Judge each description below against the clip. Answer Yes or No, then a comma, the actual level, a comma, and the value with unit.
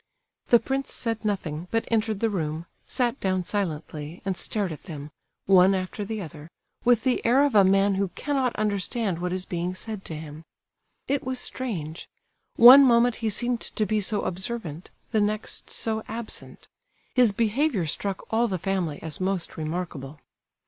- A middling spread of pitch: Yes, average, 4.8 semitones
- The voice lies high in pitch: Yes, high, 200 Hz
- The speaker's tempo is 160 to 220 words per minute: Yes, average, 165 wpm